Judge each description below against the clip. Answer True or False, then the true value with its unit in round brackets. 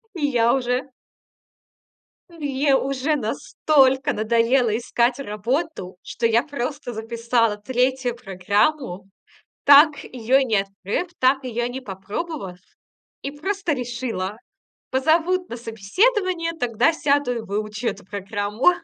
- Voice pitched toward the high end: True (250 Hz)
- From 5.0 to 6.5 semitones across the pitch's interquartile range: False (4.6 semitones)